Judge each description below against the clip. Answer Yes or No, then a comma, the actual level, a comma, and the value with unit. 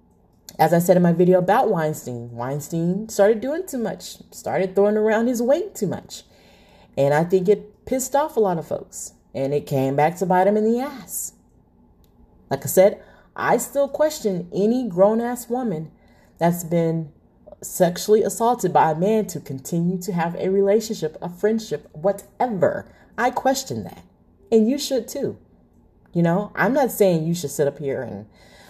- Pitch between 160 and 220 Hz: Yes, high, 190 Hz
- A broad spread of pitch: Yes, wide, 5.7 semitones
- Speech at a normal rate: Yes, average, 175 wpm